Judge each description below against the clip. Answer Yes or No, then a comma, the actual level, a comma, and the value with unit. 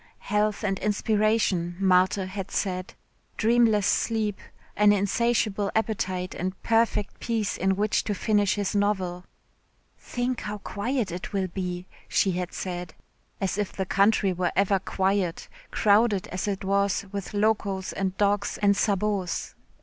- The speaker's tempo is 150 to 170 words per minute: No, average, 140 wpm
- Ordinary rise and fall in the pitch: No, narrow, 2.0 semitones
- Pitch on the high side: Yes, high, 200 Hz